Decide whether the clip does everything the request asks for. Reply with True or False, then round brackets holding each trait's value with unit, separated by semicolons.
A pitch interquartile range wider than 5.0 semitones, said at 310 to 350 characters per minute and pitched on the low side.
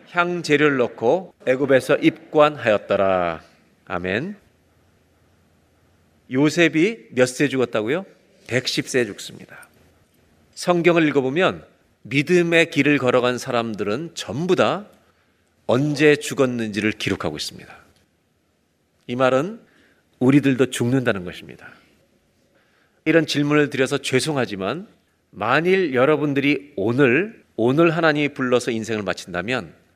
False (5.5 semitones; 245 characters per minute; 130 Hz)